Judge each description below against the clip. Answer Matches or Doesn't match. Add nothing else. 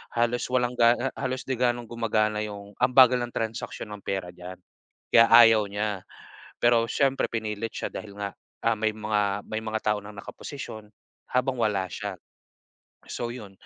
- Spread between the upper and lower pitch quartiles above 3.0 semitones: Doesn't match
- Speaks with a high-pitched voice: Doesn't match